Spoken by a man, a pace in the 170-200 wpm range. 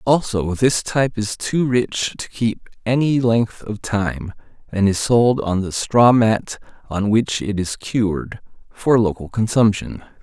No: male; average, 160 wpm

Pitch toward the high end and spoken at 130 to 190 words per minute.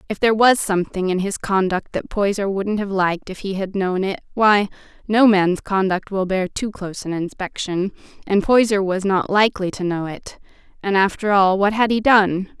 No: high, 195 Hz; average, 200 wpm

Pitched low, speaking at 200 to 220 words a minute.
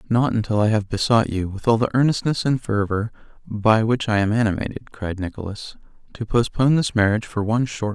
Yes: low, 110 Hz; fast, 205 wpm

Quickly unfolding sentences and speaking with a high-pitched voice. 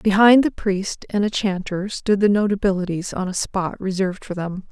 No: average, 190 wpm; high, 195 Hz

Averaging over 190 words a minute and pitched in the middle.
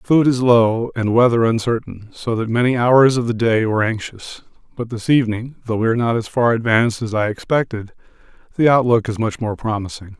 No: average, 200 wpm; low, 115 Hz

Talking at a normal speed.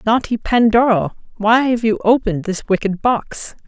Yes: average, 145 wpm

